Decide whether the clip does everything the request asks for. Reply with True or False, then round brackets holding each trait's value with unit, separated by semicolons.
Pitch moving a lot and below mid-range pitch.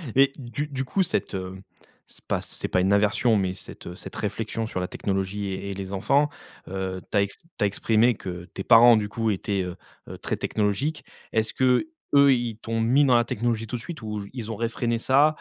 False (4.0 semitones; 110 Hz)